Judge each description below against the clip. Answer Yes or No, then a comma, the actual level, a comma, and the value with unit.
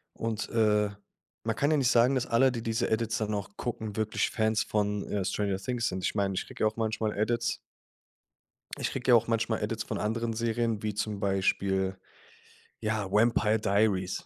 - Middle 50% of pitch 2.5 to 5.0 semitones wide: No, narrow, 2.1 semitones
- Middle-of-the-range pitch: No, low, 110 Hz